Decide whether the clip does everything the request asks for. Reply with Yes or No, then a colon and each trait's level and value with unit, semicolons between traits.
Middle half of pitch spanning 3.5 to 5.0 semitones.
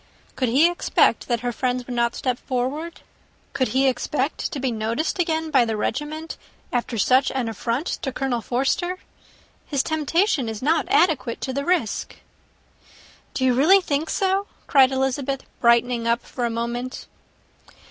Yes: average, 4.4 semitones